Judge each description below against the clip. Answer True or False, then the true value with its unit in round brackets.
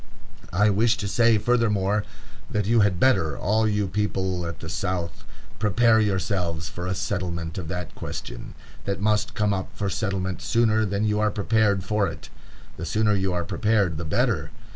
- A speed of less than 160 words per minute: False (175 wpm)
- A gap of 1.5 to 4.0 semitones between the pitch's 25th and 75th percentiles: True (3.0 semitones)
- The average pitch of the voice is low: True (100 Hz)